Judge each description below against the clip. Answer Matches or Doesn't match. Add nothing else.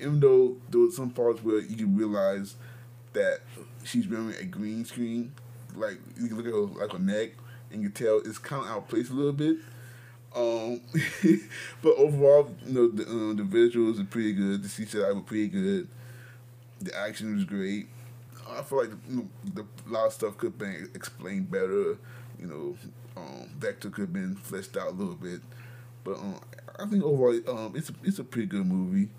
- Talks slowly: Doesn't match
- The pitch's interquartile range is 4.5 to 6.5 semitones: Matches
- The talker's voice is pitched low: Matches